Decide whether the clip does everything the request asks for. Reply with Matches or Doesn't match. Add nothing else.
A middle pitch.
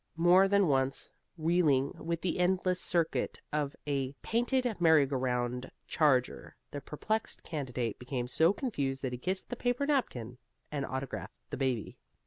Matches